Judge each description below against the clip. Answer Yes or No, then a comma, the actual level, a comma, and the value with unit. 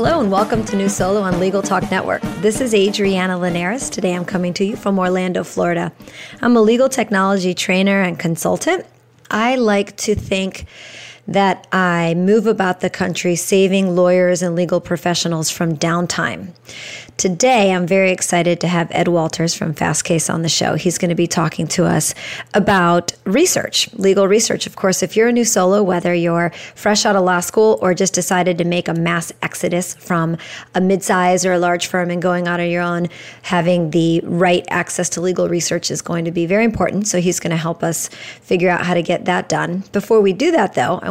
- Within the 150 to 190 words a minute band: No, average, 200 wpm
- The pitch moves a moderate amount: No, narrow, 2.1 semitones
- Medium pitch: Yes, medium, 180 Hz